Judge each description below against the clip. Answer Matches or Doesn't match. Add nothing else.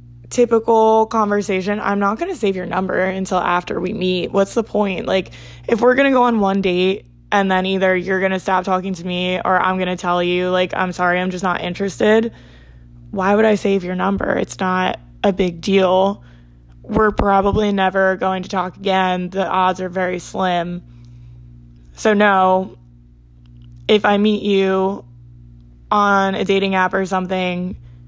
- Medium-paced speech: Matches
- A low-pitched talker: Doesn't match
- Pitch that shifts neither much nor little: Doesn't match